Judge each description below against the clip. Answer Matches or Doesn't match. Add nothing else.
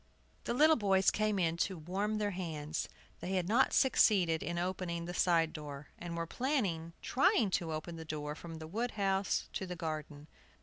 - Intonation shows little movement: Doesn't match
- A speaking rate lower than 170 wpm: Doesn't match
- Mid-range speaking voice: Matches